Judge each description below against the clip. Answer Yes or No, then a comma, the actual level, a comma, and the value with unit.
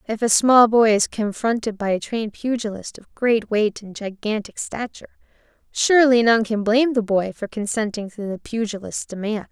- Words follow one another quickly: No, average, 175 wpm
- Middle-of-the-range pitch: No, high, 220 Hz